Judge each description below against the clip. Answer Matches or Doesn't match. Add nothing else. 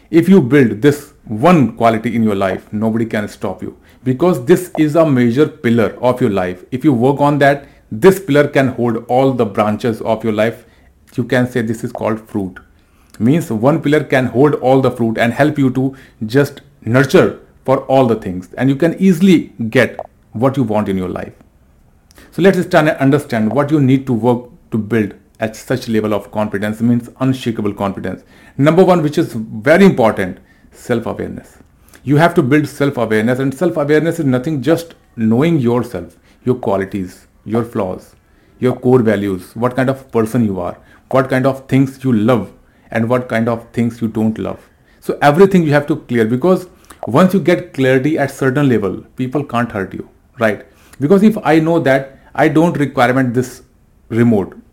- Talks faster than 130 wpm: Matches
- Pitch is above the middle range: Doesn't match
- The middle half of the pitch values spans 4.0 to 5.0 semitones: Matches